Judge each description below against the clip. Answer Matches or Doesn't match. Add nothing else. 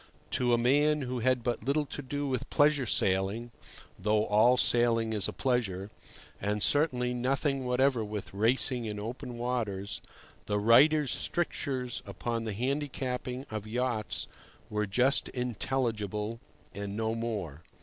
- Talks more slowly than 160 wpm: Matches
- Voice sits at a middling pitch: Doesn't match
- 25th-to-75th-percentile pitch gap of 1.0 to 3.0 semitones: Doesn't match